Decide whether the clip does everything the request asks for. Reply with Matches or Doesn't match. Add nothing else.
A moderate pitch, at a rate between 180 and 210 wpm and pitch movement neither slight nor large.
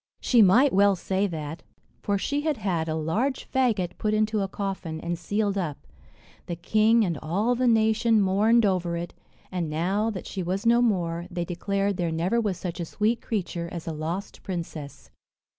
Doesn't match